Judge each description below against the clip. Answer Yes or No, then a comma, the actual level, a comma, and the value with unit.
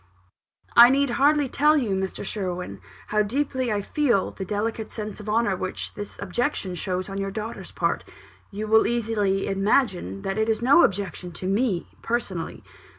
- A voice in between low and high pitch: No, high, 210 Hz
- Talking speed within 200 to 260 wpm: No, average, 165 wpm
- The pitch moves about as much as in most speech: Yes, average, 3.7 semitones